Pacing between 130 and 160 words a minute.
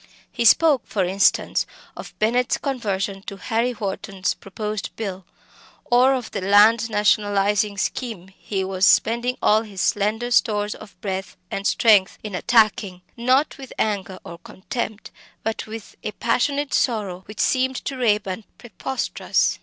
Yes: average, 140 wpm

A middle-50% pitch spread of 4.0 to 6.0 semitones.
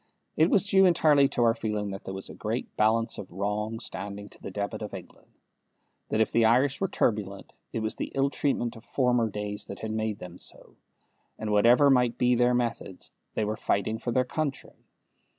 No: average, 3.3 semitones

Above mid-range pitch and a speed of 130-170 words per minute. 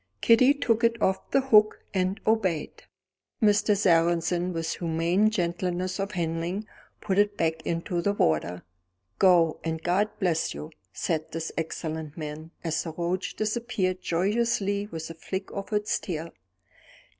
No: medium, 180 Hz; average, 145 wpm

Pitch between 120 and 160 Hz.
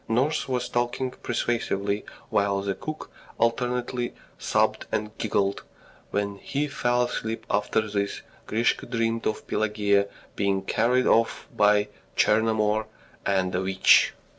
No: low, 110 Hz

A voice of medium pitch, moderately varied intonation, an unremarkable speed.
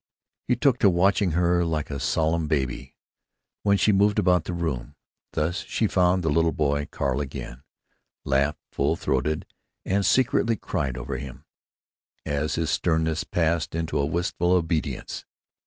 No: very low, 80 Hz; average, 3.7 semitones; average, 150 wpm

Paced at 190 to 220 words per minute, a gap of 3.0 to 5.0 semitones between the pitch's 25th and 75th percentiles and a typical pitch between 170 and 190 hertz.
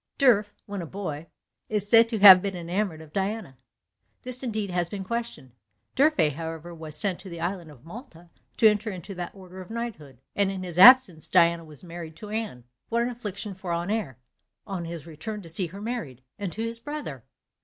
Yes: average, 195 wpm; average, 4.4 semitones; medium, 185 Hz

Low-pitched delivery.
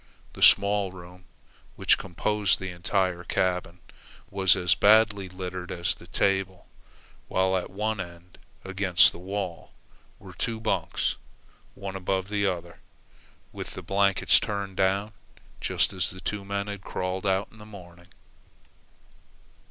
Yes: very low, 95 Hz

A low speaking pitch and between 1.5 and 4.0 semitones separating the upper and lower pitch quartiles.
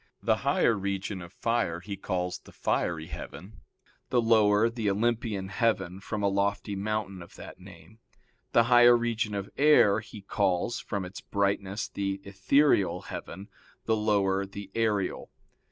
Yes: low, 100 Hz; narrow, 2.6 semitones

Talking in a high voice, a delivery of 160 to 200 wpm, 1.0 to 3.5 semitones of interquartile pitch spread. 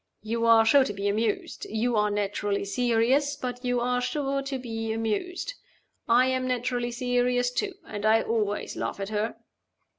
Yes: high, 240 Hz; average, 170 wpm; narrow, 2.5 semitones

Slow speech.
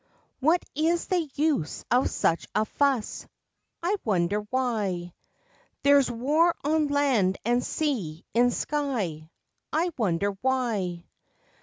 Yes: slow, 115 wpm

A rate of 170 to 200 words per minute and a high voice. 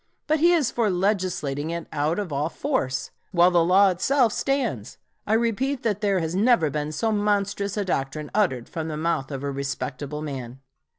No: average, 185 wpm; medium, 180 Hz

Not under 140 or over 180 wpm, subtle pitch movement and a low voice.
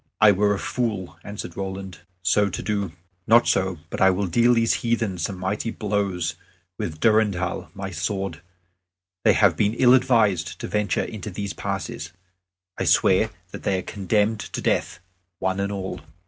Yes: average, 165 wpm; narrow, 2.3 semitones; low, 100 Hz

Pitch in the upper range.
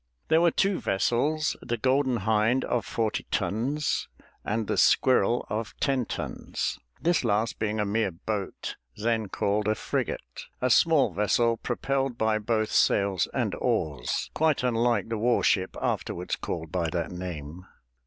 No: low, 110 Hz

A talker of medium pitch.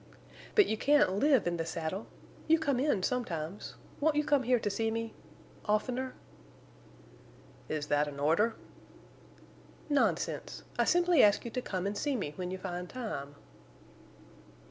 No: high, 220 Hz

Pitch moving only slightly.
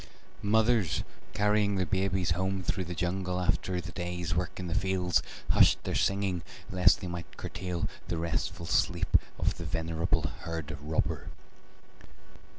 Yes: narrow, 2.2 semitones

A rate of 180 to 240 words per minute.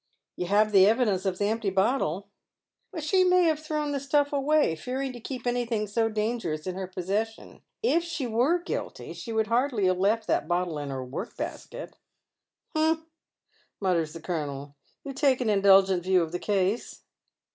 Yes: average, 190 wpm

